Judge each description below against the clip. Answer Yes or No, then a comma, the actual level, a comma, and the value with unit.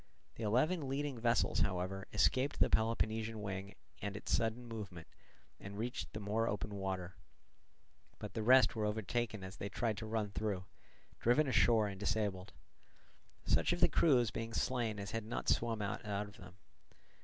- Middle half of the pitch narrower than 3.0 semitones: Yes, narrow, 2.6 semitones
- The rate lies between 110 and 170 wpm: Yes, average, 165 wpm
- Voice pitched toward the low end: Yes, low, 110 Hz